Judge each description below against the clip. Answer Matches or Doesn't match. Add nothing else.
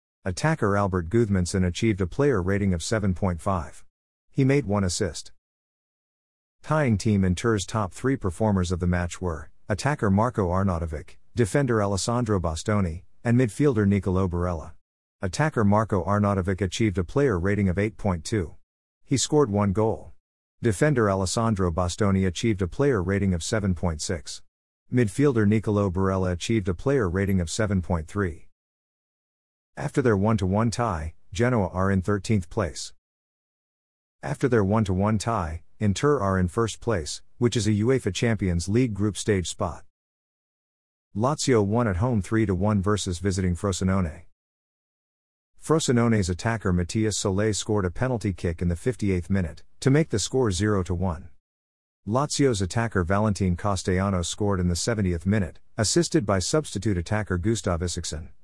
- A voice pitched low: Matches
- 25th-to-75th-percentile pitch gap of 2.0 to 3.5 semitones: Doesn't match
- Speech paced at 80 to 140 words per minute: Matches